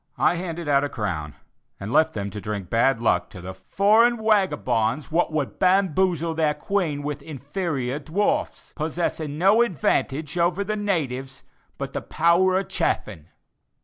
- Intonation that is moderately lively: No, wide, 6.3 semitones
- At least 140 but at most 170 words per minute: Yes, average, 150 wpm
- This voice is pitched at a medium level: Yes, medium, 155 Hz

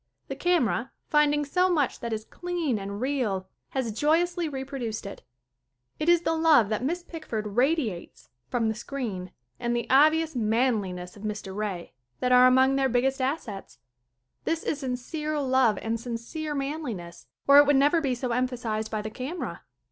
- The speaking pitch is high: Yes, very high, 255 Hz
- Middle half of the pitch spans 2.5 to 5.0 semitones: No, wide, 5.4 semitones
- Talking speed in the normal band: Yes, average, 165 wpm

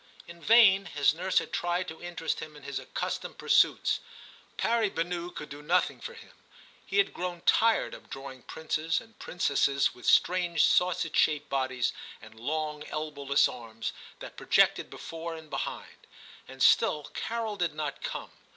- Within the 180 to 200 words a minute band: No, average, 160 wpm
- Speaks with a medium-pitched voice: Yes, medium, 160 Hz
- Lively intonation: No, average, 4.0 semitones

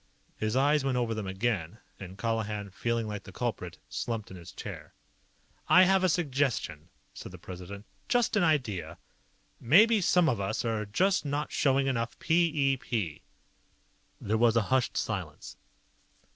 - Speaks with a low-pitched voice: Yes, low, 120 Hz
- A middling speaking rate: Yes, average, 155 wpm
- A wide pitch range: Yes, wide, 6.5 semitones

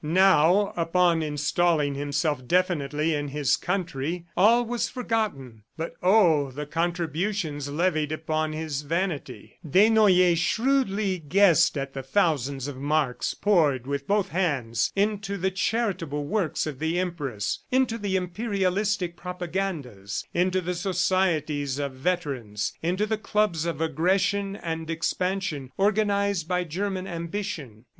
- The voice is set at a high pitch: No, medium, 170 Hz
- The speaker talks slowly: Yes, slow, 125 wpm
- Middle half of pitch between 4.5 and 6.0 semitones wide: Yes, average, 4.8 semitones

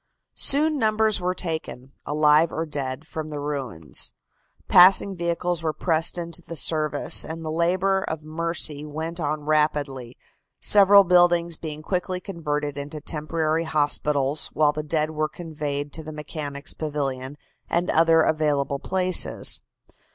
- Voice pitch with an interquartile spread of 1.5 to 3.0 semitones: Yes, narrow, 2.5 semitones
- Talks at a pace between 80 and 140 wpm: Yes, slow, 135 wpm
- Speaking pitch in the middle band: Yes, medium, 155 Hz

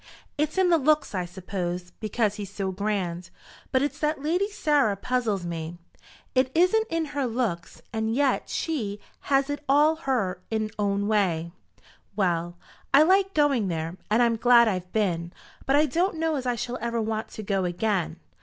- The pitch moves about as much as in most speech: No, wide, 7.4 semitones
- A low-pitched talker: No, high, 225 Hz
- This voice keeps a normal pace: Yes, average, 175 wpm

